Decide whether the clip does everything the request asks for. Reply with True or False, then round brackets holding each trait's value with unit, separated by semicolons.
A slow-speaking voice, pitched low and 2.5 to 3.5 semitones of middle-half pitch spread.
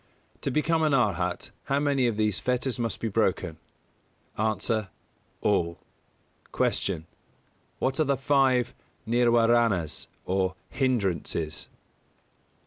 False (110 wpm; 115 Hz; 5.5 semitones)